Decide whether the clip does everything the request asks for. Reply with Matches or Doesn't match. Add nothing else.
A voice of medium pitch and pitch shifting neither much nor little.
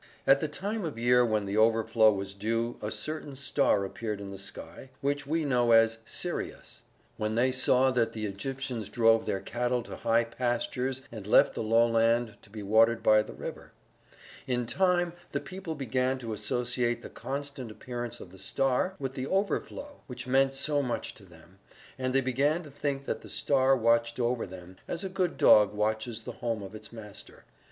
Doesn't match